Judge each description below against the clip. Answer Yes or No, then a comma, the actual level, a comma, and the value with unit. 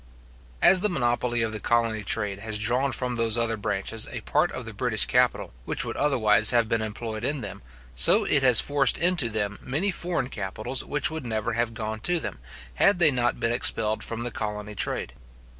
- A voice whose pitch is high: No, low, 115 Hz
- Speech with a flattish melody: No, average, 3.6 semitones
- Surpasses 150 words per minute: Yes, average, 200 wpm